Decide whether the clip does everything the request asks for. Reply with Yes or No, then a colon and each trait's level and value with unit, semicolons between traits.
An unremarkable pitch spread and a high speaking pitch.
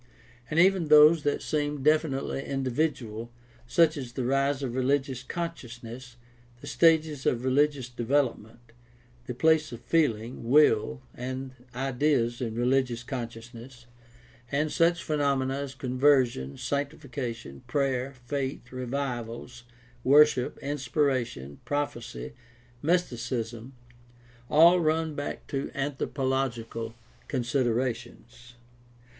No: average, 3.4 semitones; low, 130 Hz